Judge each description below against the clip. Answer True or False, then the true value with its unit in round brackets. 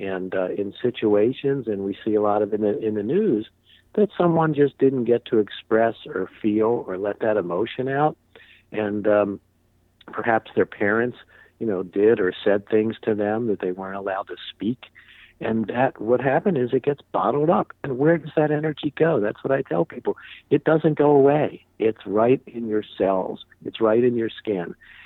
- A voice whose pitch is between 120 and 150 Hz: False (110 Hz)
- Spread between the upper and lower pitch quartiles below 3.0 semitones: False (5.0 semitones)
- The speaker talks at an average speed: True (195 wpm)